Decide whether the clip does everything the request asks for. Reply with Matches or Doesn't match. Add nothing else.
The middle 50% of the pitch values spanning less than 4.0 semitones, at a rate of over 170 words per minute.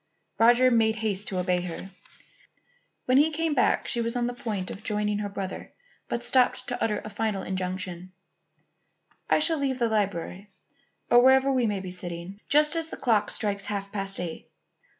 Doesn't match